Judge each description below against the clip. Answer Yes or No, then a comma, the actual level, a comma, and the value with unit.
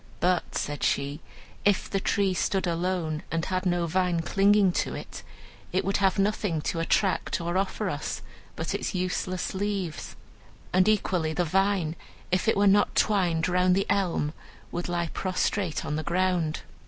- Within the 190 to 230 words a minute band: No, average, 165 wpm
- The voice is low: No, medium, 185 Hz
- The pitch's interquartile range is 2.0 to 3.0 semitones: Yes, narrow, 2.5 semitones